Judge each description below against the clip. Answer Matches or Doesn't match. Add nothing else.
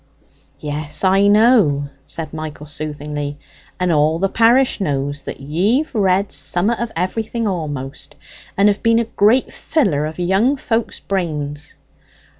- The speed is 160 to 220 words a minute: Doesn't match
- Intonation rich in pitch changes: Matches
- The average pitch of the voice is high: Doesn't match